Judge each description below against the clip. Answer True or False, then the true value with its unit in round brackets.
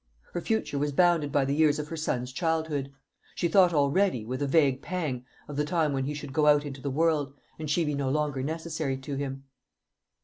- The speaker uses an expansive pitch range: False (2.7 semitones)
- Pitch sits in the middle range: True (145 Hz)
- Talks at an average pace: False (215 wpm)